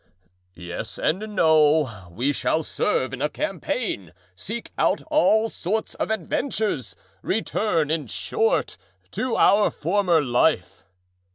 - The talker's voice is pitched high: No, medium, 160 Hz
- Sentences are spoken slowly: Yes, slow, 110 wpm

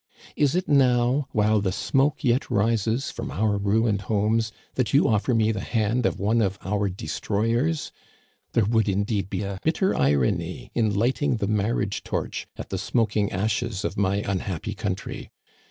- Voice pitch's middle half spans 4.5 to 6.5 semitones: No, average, 3.0 semitones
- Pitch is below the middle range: Yes, low, 110 Hz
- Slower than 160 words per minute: No, average, 165 wpm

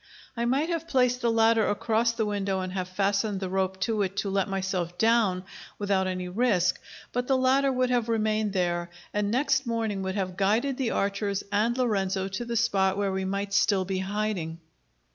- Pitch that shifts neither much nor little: Yes, average, 3.5 semitones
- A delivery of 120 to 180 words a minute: No, average, 195 wpm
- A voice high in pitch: Yes, high, 205 Hz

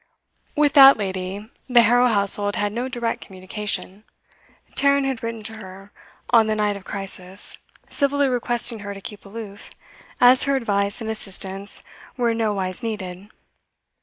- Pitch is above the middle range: Yes, high, 215 Hz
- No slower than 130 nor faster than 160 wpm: Yes, average, 150 wpm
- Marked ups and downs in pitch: No, average, 3.4 semitones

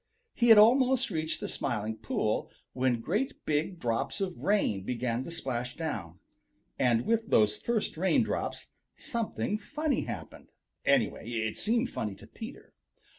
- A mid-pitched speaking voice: Yes, medium, 160 Hz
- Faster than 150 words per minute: No, average, 140 wpm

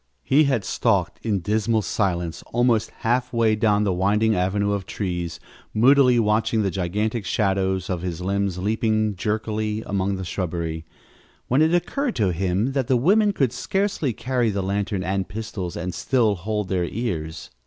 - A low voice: Yes, low, 105 Hz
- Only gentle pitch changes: No, average, 3.8 semitones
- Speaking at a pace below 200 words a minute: Yes, average, 165 wpm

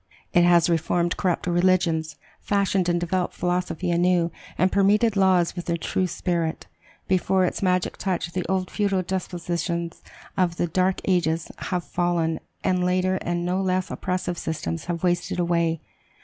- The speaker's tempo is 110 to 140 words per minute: No, average, 150 wpm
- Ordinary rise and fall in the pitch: No, narrow, 1.4 semitones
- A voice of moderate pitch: Yes, medium, 180 Hz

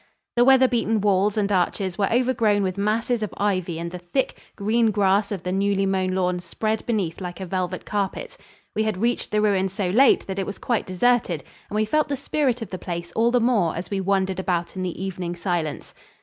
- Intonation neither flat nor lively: Yes, average, 3.1 semitones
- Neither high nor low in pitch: No, high, 200 Hz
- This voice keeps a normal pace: No, fast, 220 wpm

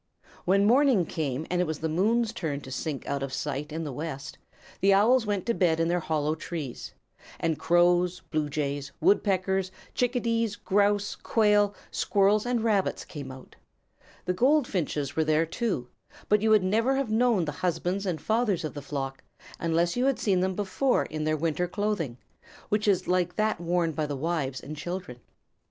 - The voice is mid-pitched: Yes, medium, 180 Hz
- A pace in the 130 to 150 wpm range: No, average, 180 wpm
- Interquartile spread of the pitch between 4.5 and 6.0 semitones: Yes, average, 5.1 semitones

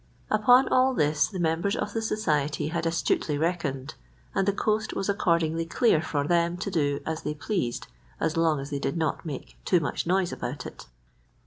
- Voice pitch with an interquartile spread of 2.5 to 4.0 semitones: No, average, 4.5 semitones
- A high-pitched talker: No, medium, 165 Hz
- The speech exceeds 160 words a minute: Yes, average, 190 wpm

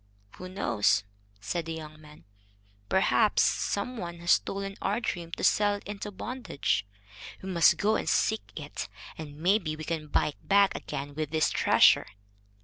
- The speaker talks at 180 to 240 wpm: No, average, 165 wpm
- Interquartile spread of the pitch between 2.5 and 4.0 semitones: No, average, 4.8 semitones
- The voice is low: No, medium, 170 Hz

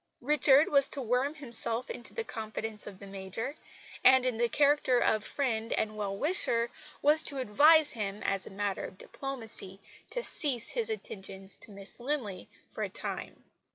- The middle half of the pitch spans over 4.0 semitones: Yes, wide, 5.5 semitones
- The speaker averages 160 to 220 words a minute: Yes, average, 170 wpm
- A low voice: No, high, 235 Hz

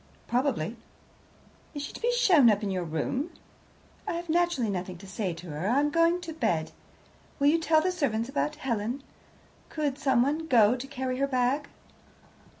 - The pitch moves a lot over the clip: Yes, wide, 6.1 semitones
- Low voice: No, very high, 270 Hz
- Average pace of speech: Yes, average, 175 wpm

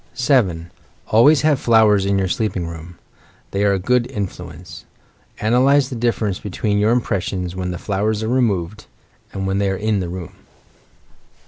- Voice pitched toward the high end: No, low, 100 Hz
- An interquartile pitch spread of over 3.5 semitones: Yes, average, 4.1 semitones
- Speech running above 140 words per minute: Yes, average, 160 wpm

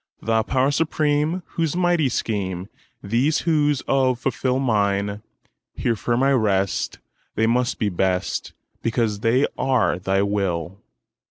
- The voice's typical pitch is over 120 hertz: No, low, 115 Hz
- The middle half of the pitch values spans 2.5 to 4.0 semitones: No, wide, 5.5 semitones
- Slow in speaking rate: Yes, slow, 110 wpm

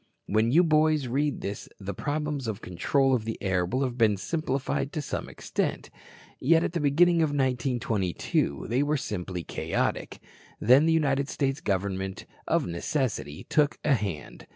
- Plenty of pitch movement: Yes, wide, 6.6 semitones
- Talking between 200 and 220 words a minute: No, average, 160 wpm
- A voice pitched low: Yes, low, 130 Hz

